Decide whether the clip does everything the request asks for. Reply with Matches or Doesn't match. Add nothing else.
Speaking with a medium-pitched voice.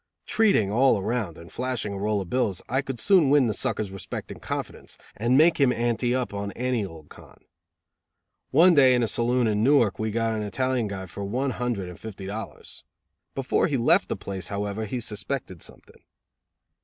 Doesn't match